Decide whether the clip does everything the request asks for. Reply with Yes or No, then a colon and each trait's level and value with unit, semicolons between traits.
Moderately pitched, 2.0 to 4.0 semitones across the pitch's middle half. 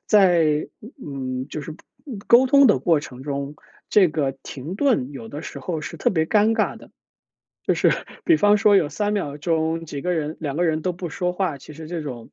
No: medium, 160 Hz; average, 4.5 semitones